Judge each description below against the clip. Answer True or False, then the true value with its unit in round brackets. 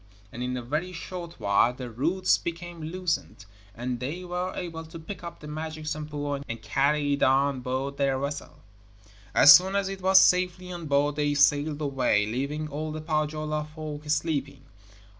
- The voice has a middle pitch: True (150 Hz)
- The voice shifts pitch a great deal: False (3.1 semitones)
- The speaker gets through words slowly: False (175 wpm)